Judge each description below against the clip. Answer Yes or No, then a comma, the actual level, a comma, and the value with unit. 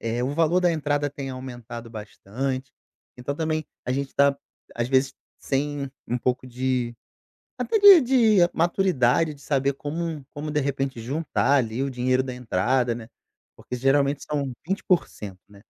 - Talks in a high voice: No, low, 135 Hz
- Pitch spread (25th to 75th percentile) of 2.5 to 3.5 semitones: Yes, average, 3.1 semitones